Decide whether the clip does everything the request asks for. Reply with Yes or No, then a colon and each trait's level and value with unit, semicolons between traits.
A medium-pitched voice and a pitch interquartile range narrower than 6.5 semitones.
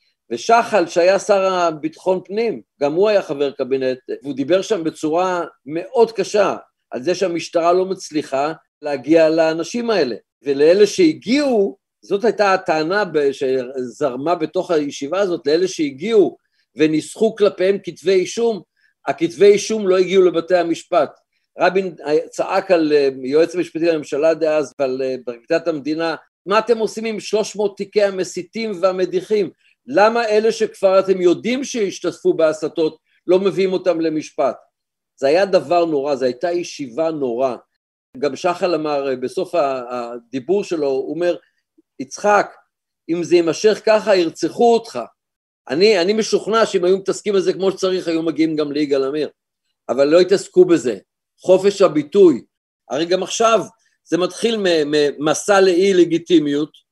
Yes: medium, 180 Hz; average, 5.1 semitones